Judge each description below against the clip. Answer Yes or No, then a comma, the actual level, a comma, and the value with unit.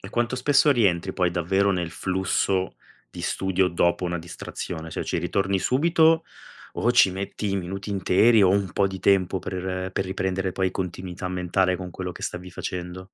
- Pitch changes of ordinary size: No, narrow, 1.5 semitones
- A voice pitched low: Yes, very low, 95 Hz